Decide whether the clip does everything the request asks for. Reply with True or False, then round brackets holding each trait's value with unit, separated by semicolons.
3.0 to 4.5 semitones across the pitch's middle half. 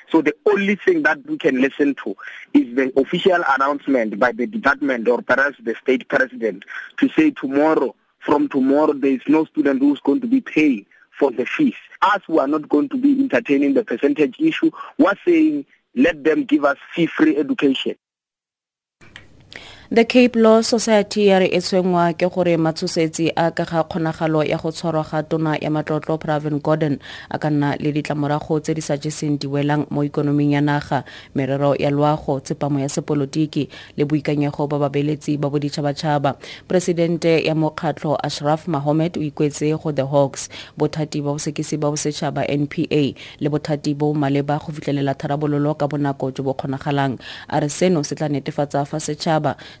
False (2.5 semitones)